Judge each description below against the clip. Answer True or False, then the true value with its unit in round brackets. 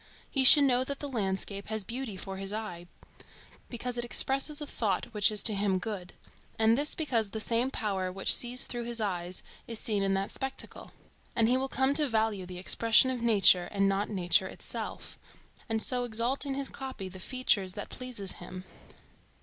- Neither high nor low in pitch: False (220 Hz)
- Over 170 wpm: True (190 wpm)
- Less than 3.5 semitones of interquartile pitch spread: False (4.5 semitones)